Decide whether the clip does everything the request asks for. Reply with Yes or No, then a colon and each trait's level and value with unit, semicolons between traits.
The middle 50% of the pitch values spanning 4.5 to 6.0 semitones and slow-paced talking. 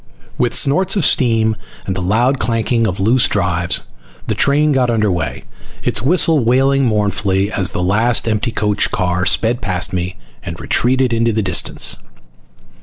No: average, 5.0 semitones; average, 165 wpm